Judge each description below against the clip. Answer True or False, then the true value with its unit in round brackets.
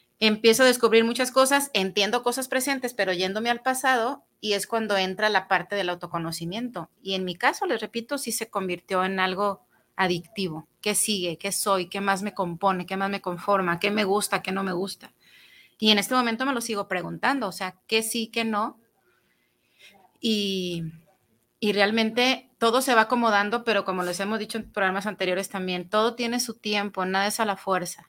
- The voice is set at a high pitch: True (205 Hz)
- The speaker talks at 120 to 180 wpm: False (190 wpm)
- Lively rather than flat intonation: False (3.4 semitones)